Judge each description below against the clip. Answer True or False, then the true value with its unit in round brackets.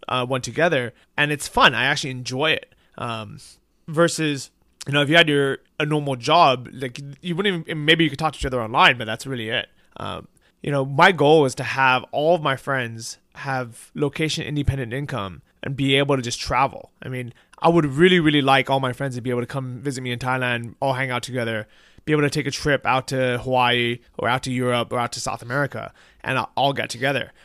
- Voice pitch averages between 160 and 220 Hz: False (135 Hz)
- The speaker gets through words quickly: True (225 wpm)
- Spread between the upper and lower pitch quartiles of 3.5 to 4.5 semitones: False (3.0 semitones)